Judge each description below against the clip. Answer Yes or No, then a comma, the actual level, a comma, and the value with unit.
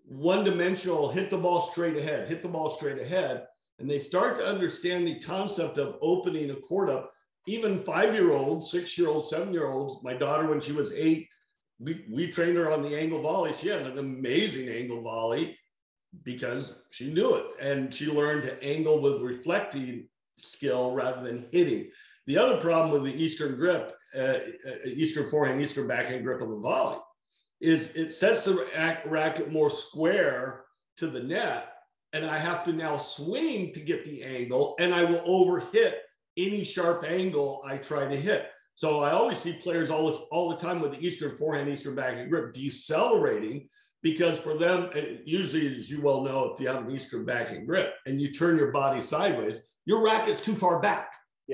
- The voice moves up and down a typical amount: Yes, average, 4.1 semitones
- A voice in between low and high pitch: Yes, medium, 160 Hz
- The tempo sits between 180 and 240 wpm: Yes, average, 190 wpm